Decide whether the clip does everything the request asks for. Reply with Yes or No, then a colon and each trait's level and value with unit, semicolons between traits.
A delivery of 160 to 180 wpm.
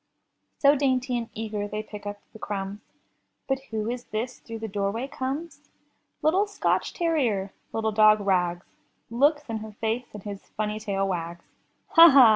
Yes: average, 165 wpm